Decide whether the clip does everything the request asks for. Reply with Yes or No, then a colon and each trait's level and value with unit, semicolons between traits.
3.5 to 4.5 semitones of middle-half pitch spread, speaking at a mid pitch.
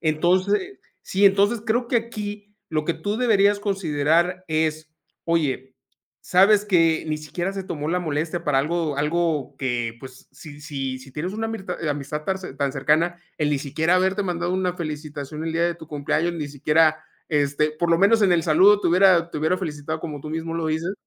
Yes: average, 3.8 semitones; medium, 165 Hz